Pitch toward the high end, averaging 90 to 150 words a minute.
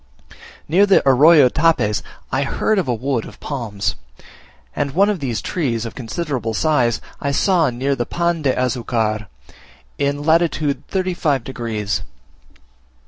No: medium, 140 Hz; average, 140 wpm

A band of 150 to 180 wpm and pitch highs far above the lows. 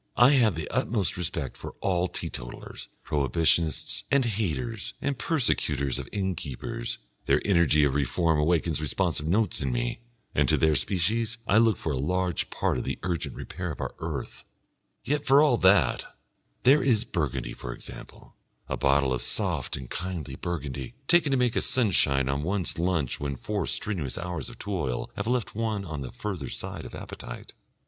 Yes: average, 170 wpm; wide, 7.1 semitones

